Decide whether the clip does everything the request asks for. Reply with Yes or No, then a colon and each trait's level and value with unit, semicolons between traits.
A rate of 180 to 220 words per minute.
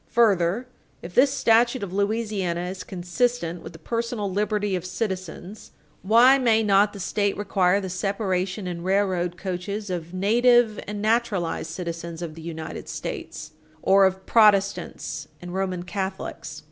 No: average, 145 wpm